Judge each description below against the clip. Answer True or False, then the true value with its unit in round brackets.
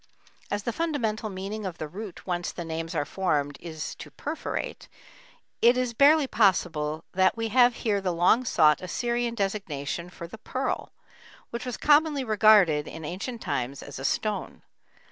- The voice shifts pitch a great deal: True (6.2 semitones)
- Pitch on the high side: True (200 Hz)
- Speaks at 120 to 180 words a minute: True (165 wpm)